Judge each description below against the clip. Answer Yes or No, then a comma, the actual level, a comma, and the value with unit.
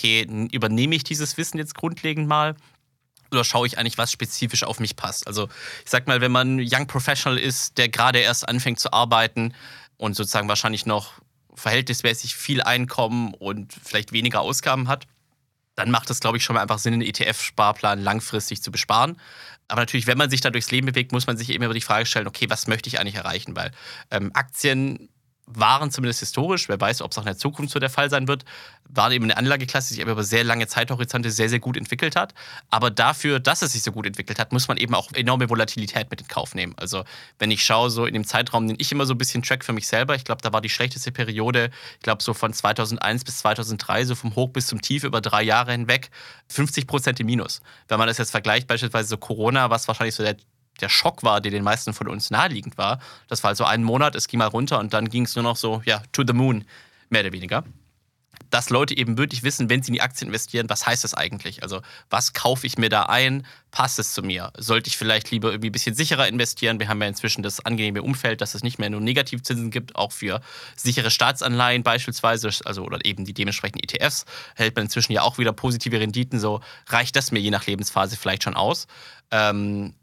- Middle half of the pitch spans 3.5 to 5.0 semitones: No, average, 2.8 semitones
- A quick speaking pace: Yes, fast, 230 wpm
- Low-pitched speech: Yes, low, 120 Hz